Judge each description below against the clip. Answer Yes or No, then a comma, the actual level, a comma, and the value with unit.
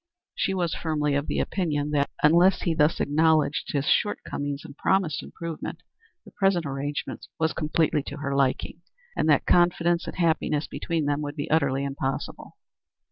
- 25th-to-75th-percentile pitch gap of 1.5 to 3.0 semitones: Yes, average, 2.7 semitones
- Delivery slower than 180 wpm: Yes, average, 160 wpm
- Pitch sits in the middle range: Yes, medium, 155 Hz